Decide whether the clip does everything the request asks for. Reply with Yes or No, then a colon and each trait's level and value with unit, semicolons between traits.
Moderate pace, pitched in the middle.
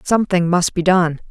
Yes: average, 185 wpm; medium, 180 Hz